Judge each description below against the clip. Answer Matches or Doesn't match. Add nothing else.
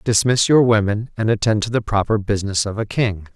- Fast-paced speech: Matches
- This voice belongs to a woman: Doesn't match